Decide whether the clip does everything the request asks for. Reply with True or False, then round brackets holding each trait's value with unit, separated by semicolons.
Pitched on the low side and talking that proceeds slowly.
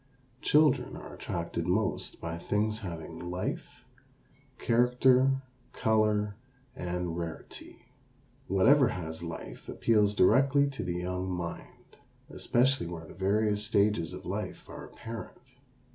True (105 Hz; 115 wpm)